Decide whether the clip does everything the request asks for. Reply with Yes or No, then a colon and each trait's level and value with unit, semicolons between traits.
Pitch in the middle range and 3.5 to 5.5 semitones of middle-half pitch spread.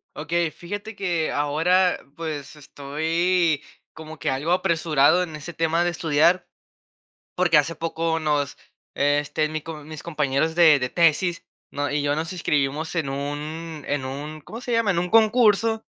No: medium, 160 Hz; average, 2.9 semitones